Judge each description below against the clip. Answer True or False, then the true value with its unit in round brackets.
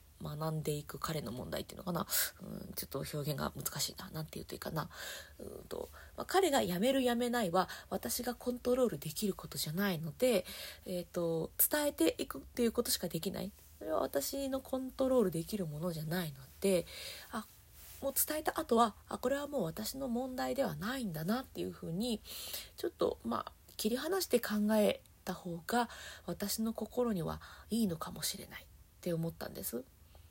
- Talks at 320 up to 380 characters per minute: True (375 characters per minute)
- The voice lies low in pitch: False (205 Hz)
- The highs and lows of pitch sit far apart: True (7.0 semitones)